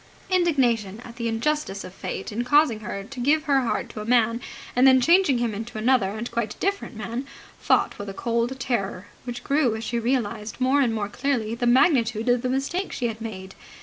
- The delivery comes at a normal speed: No, fast, 210 wpm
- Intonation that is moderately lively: Yes, average, 3.3 semitones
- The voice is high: Yes, high, 240 Hz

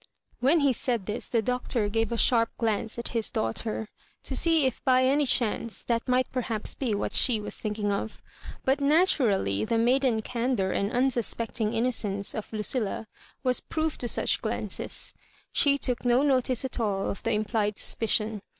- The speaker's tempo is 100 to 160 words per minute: No, average, 170 wpm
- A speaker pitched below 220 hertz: No, high, 235 Hz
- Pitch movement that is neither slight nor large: Yes, average, 3.2 semitones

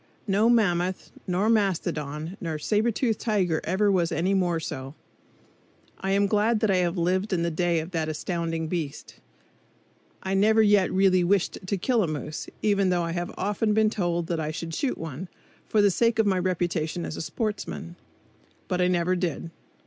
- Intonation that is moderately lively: Yes, average, 3.4 semitones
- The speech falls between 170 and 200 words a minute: Yes, average, 180 wpm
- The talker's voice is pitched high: No, medium, 180 Hz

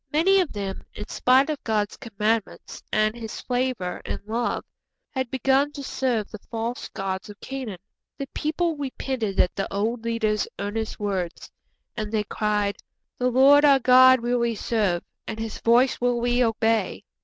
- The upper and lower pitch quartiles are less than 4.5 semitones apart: Yes, average, 3.5 semitones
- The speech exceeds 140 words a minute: Yes, average, 165 wpm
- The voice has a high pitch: Yes, high, 230 Hz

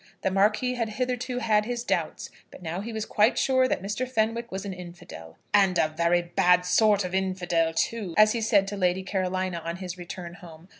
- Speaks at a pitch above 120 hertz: Yes, high, 190 Hz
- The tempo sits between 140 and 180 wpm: No, fast, 205 wpm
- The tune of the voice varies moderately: Yes, average, 3.7 semitones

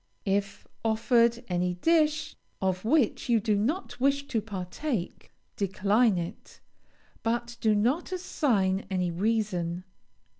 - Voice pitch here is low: No, high, 220 Hz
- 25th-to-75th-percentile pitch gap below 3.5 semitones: No, average, 4.7 semitones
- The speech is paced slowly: Yes, slow, 115 wpm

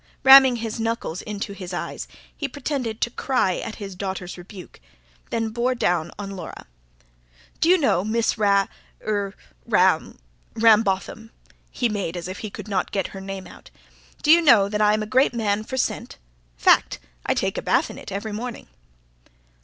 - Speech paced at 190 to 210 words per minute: No, average, 165 wpm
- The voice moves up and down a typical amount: Yes, average, 3.3 semitones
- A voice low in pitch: No, high, 210 Hz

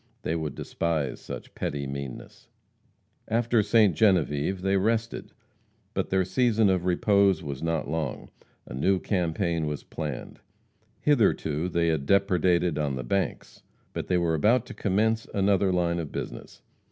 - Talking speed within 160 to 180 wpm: No, average, 145 wpm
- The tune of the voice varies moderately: Yes, average, 4.2 semitones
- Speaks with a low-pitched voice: Yes, very low, 90 Hz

